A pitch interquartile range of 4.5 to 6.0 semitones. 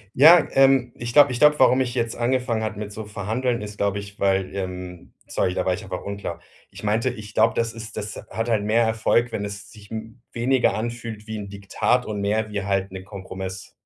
No: average, 2.8 semitones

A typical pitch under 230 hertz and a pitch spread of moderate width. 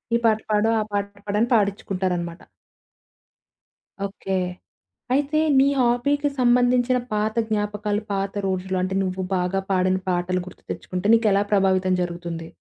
Yes: high, 200 Hz; average, 3.4 semitones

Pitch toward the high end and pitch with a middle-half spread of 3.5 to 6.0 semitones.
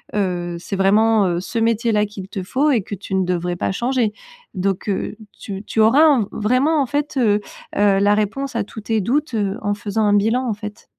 No: high, 210 Hz; average, 3.1 semitones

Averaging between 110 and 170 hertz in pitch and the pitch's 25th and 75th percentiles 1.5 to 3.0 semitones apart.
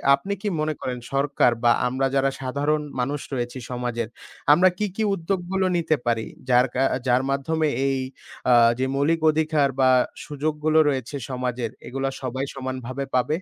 No: low, 135 Hz; average, 3.4 semitones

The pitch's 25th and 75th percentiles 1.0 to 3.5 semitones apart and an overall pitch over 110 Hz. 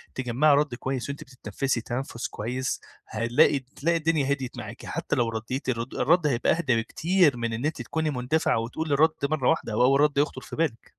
No: average, 3.9 semitones; low, 135 Hz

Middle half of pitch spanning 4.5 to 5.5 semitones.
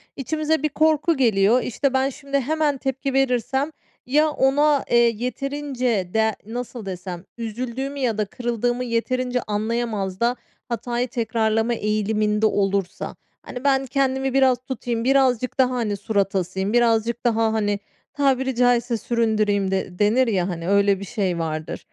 No: average, 3.9 semitones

